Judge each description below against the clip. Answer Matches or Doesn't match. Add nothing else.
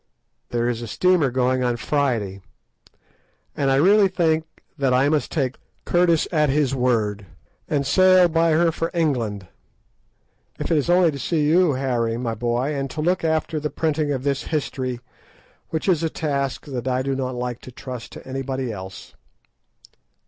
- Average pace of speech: Matches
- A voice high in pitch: Doesn't match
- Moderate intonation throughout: Matches